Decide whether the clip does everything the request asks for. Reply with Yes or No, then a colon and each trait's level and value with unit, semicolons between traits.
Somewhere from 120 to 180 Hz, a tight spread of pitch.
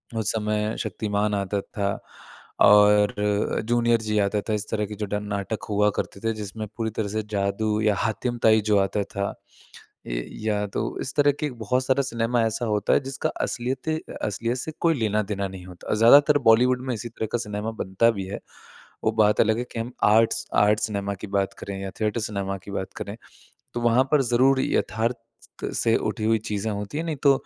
No: low, 110 Hz; narrow, 2.3 semitones